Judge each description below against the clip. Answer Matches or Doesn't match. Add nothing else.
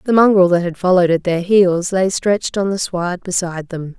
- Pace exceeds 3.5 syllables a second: Matches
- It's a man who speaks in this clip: Doesn't match